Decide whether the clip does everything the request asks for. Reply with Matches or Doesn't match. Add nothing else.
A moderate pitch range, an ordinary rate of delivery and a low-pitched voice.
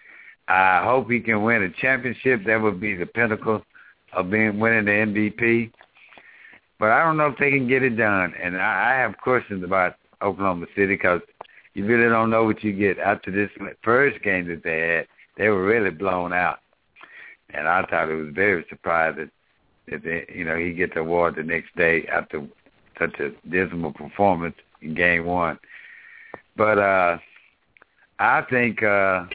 Matches